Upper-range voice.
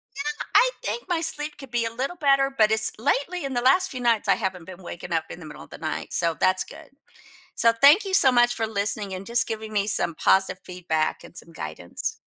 Yes: high, 225 Hz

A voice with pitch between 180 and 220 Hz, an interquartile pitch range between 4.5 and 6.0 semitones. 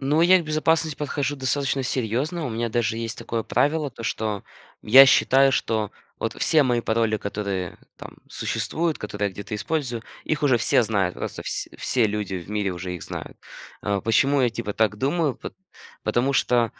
No: low, 120 Hz; average, 5.0 semitones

